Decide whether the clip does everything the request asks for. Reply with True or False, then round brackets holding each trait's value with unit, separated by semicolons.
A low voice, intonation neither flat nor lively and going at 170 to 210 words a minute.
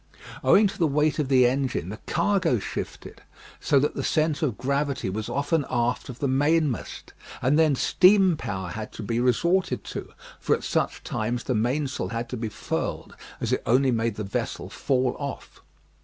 True (130 Hz; 4.5 semitones; 185 wpm)